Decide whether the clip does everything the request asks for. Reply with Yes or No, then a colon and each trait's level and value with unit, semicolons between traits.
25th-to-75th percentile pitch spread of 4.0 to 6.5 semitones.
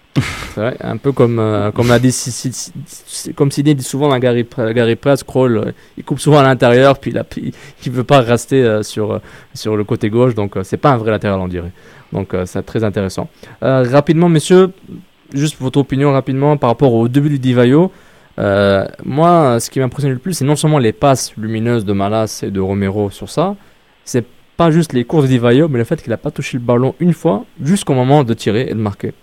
Yes: average, 4.7 semitones